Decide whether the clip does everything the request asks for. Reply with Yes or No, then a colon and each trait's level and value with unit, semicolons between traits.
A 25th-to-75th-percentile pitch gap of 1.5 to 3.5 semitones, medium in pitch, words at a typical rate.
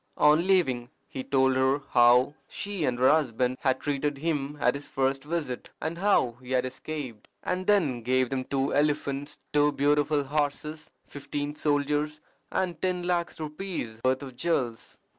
Yes: average, 2.9 semitones; medium, 145 Hz; average, 160 wpm